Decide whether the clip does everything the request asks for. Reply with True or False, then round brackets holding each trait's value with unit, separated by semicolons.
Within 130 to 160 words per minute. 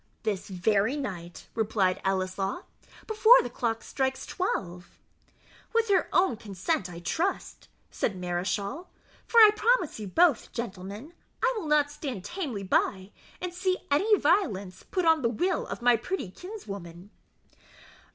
True (140 wpm)